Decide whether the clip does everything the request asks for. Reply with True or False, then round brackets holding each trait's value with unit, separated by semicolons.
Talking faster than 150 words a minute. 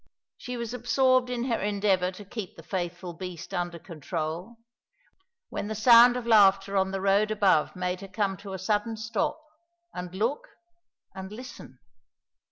True (160 wpm)